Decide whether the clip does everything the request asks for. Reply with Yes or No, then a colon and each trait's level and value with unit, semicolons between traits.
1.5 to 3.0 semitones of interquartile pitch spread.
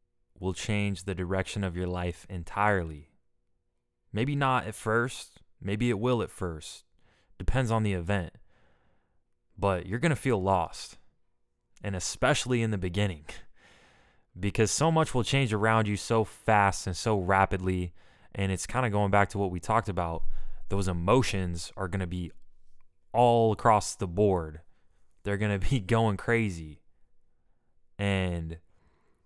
No: average, 3.7 semitones